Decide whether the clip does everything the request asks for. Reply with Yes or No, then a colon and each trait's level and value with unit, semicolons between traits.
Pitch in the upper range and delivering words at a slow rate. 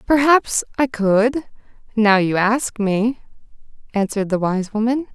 Yes: high, 225 Hz; slow, 130 wpm